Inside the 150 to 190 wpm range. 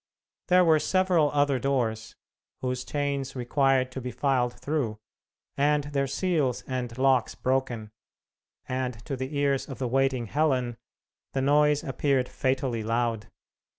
No: slow, 135 wpm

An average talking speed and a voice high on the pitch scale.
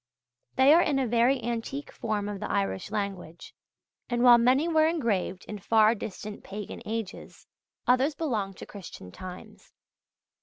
Yes: average, 150 wpm; high, 225 Hz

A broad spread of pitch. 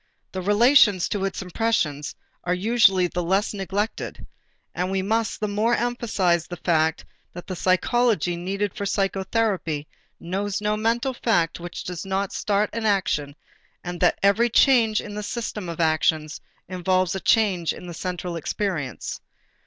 No: average, 3.3 semitones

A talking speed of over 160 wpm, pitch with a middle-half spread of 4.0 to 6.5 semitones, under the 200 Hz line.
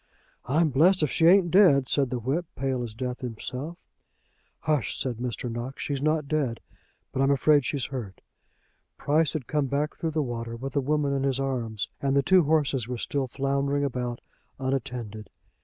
No: average, 185 wpm; average, 3.2 semitones; low, 135 Hz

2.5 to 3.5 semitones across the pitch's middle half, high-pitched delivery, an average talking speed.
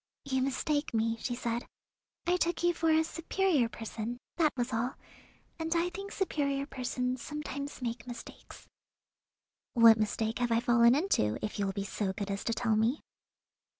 No: average, 5.1 semitones; very high, 250 Hz; average, 170 wpm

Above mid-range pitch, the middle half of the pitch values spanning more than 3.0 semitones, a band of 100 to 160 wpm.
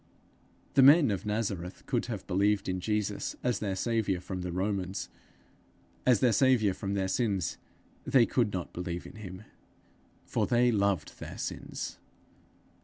No: low, 100 Hz; average, 3.6 semitones; average, 150 wpm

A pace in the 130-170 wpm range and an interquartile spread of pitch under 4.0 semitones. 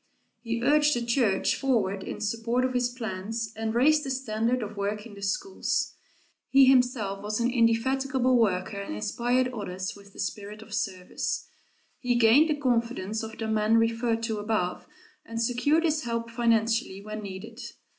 Yes: average, 165 wpm; average, 2.9 semitones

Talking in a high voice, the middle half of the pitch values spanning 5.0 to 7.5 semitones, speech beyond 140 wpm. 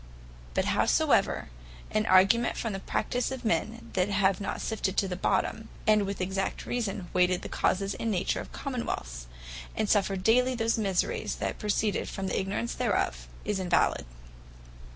No: high, 200 Hz; average, 3.1 semitones; average, 165 wpm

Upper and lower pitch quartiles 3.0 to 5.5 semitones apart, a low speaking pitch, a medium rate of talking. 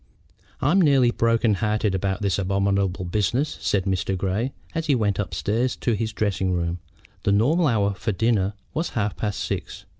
Yes: average, 3.4 semitones; low, 105 Hz; average, 170 wpm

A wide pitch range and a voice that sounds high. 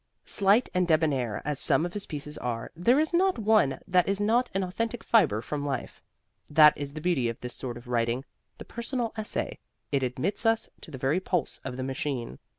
No: wide, 7.9 semitones; medium, 155 Hz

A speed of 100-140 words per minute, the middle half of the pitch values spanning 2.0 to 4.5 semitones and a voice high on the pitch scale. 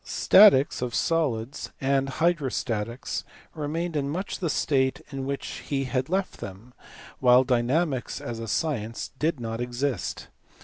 No: slow, 135 wpm; average, 4.1 semitones; low, 135 Hz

